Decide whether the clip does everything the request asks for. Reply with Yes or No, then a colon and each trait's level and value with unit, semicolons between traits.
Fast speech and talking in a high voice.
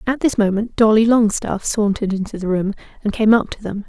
Yes: fast, 215 wpm; high, 210 Hz